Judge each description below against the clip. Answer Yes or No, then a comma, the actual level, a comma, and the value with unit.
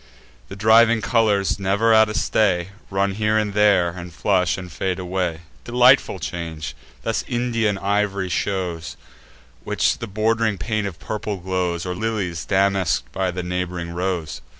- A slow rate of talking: No, average, 150 wpm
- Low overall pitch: Yes, very low, 95 Hz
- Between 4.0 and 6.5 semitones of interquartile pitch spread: No, average, 3.3 semitones